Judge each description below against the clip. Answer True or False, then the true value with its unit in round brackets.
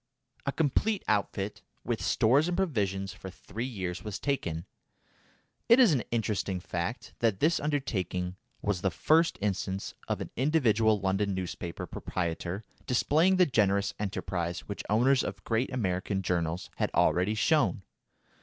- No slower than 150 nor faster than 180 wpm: False (140 wpm)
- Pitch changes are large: True (5.9 semitones)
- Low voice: True (105 Hz)